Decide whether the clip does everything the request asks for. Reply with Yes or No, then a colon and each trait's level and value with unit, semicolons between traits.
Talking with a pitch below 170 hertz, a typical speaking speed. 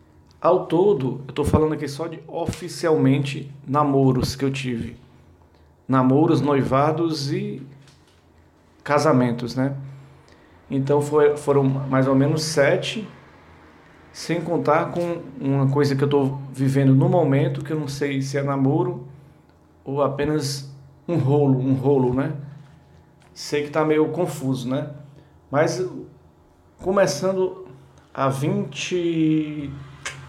No: medium, 140 Hz; slow, 120 wpm